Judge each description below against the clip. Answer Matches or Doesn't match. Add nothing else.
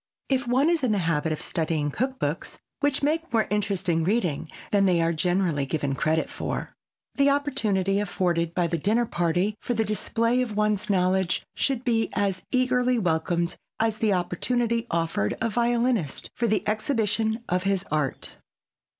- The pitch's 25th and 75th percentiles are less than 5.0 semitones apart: Doesn't match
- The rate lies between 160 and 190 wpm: Matches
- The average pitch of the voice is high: Matches